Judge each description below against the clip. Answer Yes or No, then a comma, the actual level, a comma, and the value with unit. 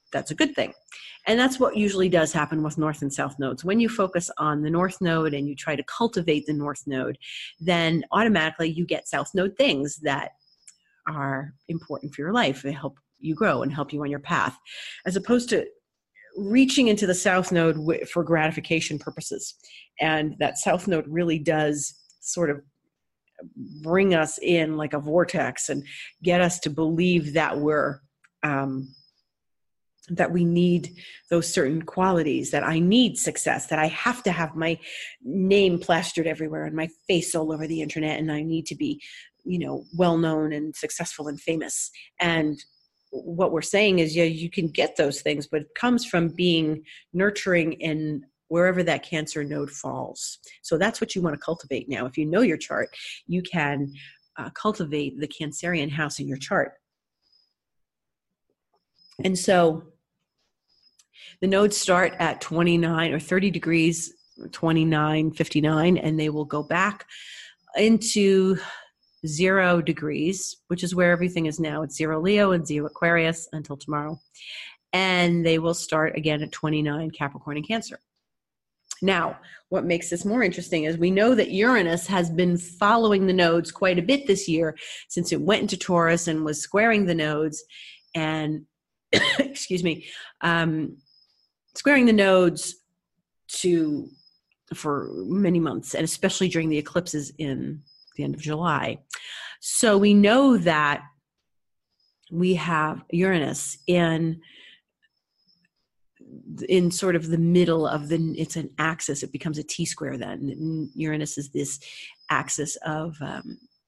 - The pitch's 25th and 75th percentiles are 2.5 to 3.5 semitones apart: Yes, average, 3.0 semitones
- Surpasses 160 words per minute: No, average, 155 wpm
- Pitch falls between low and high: Yes, medium, 165 Hz